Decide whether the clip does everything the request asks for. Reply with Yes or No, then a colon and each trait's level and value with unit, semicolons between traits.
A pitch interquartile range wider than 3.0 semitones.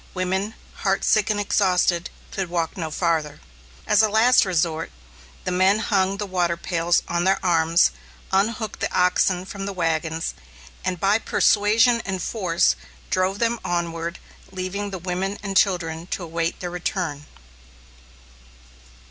No: average, 2.7 semitones